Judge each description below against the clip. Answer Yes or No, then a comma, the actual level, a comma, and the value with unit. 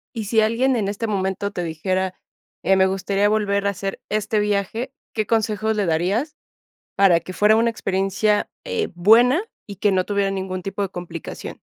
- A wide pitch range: No, narrow, 2.4 semitones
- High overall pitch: Yes, high, 200 Hz